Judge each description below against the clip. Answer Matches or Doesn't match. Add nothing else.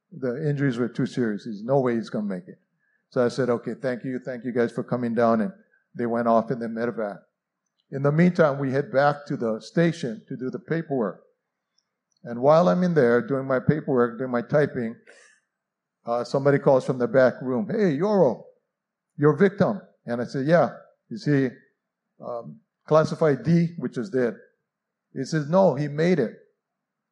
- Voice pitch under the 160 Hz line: Matches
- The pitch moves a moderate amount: Doesn't match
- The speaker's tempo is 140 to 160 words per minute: Doesn't match